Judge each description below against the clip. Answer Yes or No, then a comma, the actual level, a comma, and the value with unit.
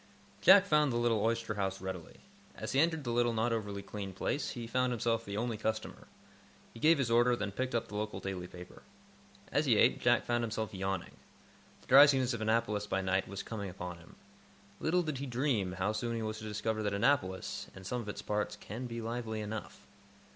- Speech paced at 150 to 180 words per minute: No, fast, 205 wpm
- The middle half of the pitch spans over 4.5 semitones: No, average, 3.1 semitones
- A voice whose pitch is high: No, low, 110 Hz